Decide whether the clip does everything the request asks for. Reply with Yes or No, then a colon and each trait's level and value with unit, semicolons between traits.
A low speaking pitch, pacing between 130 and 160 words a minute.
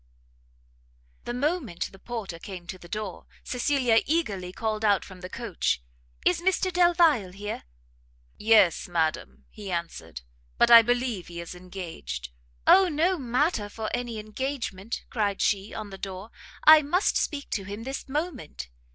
No: high, 215 Hz; average, 150 wpm